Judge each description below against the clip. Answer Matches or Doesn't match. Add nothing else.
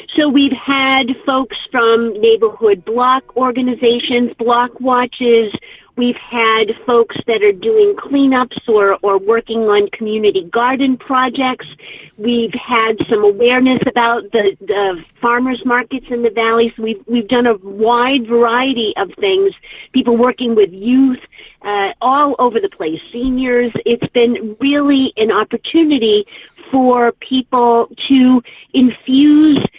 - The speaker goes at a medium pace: Doesn't match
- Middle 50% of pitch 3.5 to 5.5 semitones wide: Doesn't match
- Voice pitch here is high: Matches